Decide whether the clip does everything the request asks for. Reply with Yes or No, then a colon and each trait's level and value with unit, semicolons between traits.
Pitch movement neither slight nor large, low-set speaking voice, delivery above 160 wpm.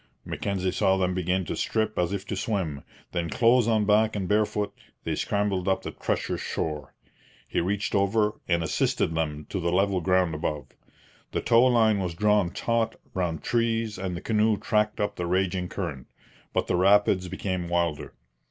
Yes: average, 3.3 semitones; very low, 95 Hz; average, 175 wpm